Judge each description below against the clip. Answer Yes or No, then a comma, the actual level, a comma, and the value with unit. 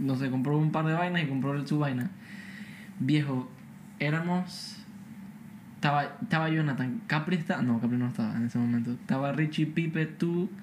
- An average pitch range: No, wide, 5.9 semitones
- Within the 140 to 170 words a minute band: Yes, average, 165 wpm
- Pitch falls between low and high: Yes, medium, 160 Hz